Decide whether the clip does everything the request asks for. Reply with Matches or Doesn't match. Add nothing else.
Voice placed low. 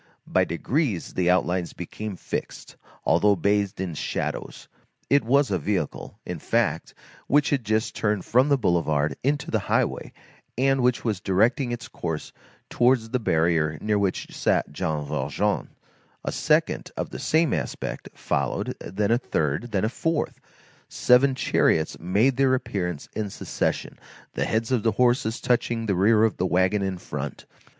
Matches